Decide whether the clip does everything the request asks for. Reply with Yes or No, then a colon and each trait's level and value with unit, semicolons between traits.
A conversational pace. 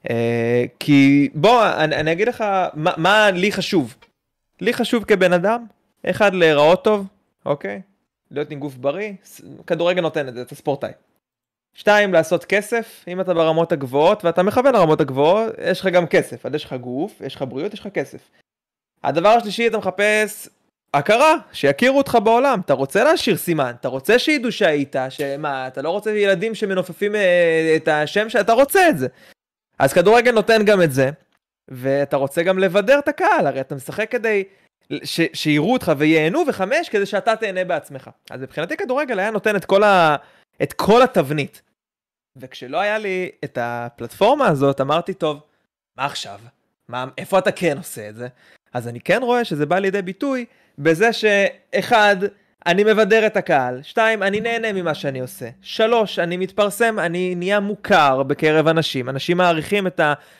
No: fast, 165 wpm